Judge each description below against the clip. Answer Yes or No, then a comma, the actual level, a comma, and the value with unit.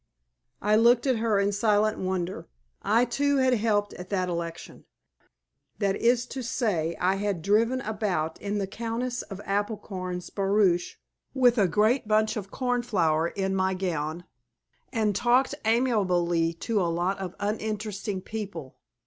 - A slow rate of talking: No, average, 145 wpm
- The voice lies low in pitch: No, high, 205 Hz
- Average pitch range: Yes, average, 3.8 semitones